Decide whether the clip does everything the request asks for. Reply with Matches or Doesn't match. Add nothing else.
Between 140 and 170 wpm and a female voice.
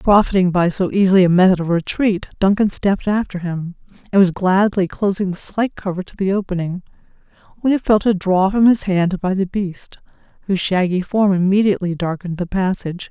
Doesn't match